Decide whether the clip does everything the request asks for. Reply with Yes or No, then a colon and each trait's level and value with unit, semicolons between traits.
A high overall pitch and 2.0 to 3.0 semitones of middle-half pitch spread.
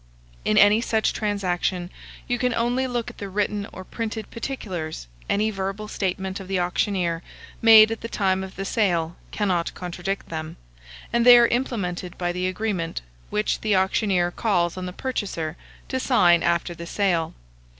No: high, 195 Hz; average, 3.7 semitones